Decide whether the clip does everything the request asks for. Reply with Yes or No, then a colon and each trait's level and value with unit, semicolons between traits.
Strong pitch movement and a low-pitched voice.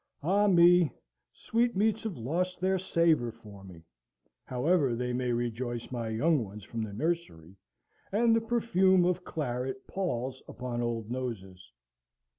Yes: wide, 7.7 semitones; low, 130 Hz